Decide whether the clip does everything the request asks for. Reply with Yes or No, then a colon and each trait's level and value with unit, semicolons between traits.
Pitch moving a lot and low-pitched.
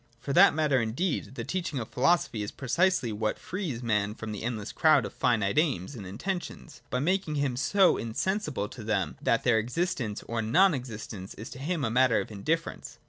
Yes: wide, 6.8 semitones; low, 125 Hz